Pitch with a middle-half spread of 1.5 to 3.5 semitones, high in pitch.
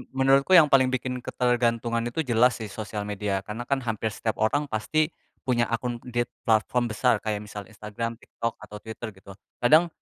No: average, 2.7 semitones; low, 115 Hz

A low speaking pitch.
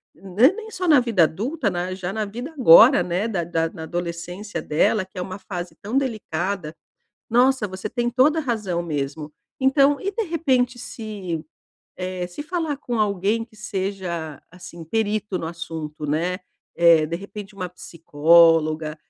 No: high, 190 Hz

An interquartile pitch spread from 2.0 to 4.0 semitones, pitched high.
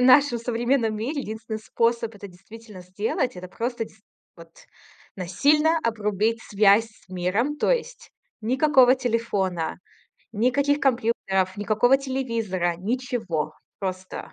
No: average, 4.4 semitones; high, 225 Hz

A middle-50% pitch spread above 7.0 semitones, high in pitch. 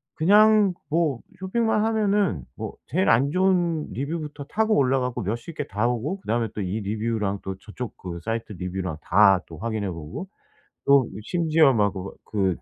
No: wide, 8.8 semitones; low, 125 Hz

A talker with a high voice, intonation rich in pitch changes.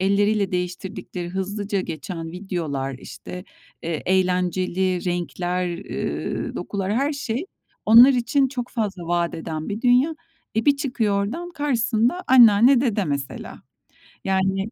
No: high, 200 Hz; average, 5.0 semitones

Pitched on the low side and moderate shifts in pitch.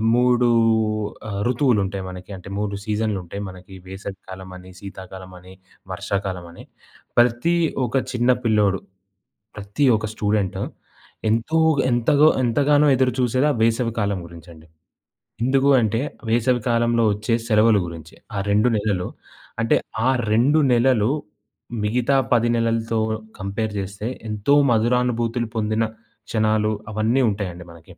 Yes: low, 110 Hz; average, 3.4 semitones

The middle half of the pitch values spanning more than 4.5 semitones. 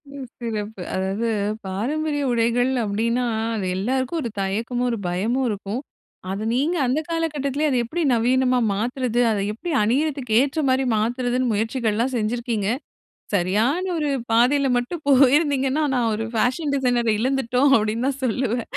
No: average, 3.5 semitones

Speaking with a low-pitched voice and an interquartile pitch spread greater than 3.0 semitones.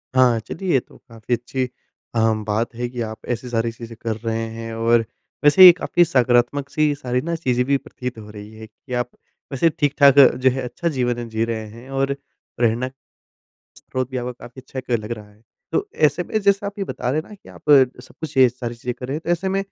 Yes: low, 125 Hz; average, 3.6 semitones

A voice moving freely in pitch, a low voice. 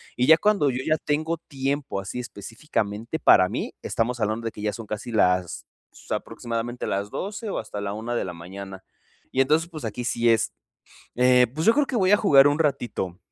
Yes: wide, 6.4 semitones; low, 120 Hz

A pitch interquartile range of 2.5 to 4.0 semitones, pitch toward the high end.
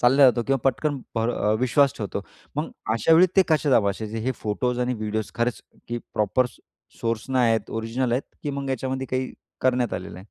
No: average, 2.9 semitones; low, 125 Hz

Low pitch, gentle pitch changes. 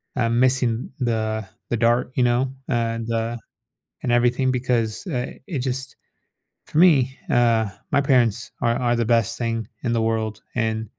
Yes: low, 120 Hz; narrow, 1.8 semitones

